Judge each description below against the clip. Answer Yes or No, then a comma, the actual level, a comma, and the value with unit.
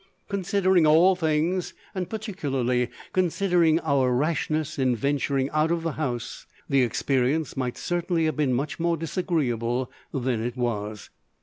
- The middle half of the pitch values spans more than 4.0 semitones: Yes, average, 5.1 semitones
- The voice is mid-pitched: Yes, medium, 155 Hz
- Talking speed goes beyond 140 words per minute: No, slow, 135 wpm